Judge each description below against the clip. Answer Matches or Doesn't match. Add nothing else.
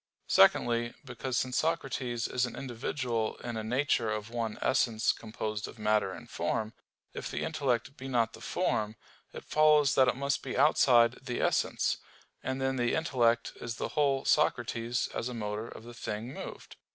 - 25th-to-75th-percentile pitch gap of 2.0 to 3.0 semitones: Matches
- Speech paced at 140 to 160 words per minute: Doesn't match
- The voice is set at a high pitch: Doesn't match